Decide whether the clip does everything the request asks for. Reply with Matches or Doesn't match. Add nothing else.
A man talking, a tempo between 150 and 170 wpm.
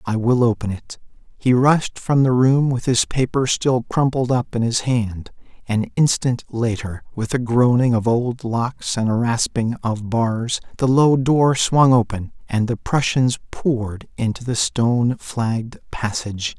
Matches